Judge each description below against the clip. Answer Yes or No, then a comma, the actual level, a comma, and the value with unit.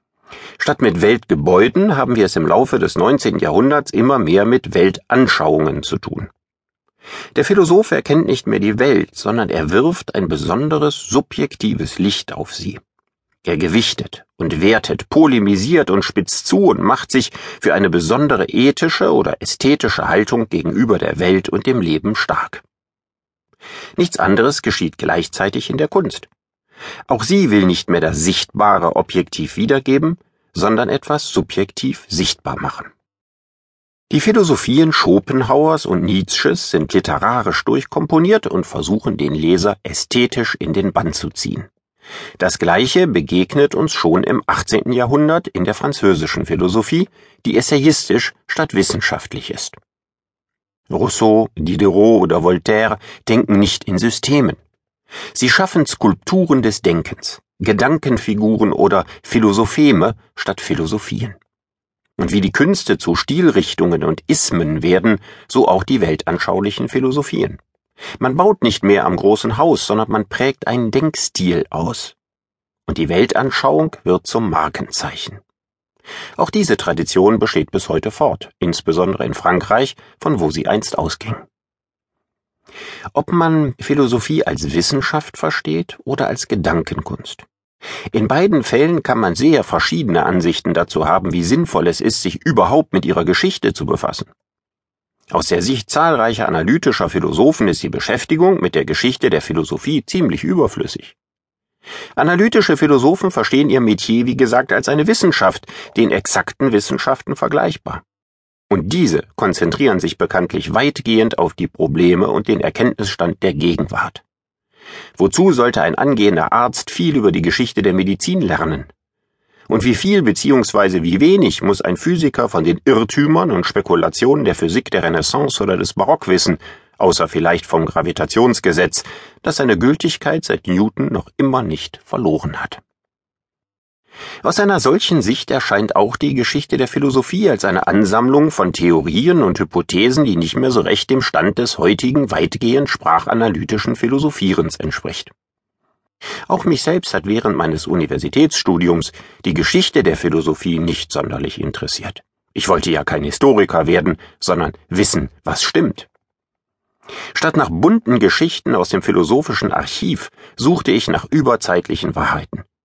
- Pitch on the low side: Yes, low, 115 Hz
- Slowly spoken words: No, average, 135 wpm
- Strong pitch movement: Yes, wide, 7.0 semitones